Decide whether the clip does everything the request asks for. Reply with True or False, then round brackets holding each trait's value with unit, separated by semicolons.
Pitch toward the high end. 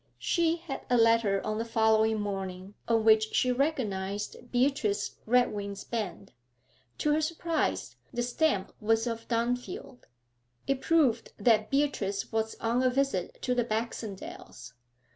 True (230 Hz)